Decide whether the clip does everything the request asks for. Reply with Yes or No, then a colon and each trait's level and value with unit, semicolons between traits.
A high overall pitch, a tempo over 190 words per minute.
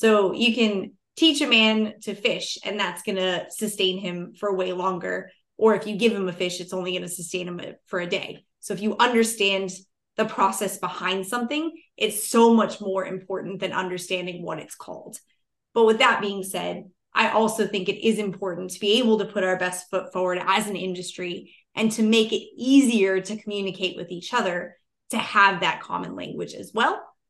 Yes: high, 195 Hz; average, 200 wpm